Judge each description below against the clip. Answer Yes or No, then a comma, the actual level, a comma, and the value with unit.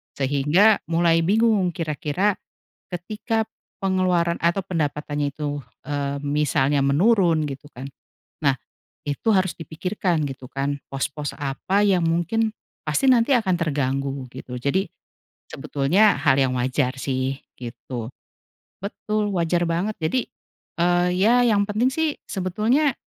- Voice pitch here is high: No, medium, 165 Hz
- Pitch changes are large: Yes, wide, 6.1 semitones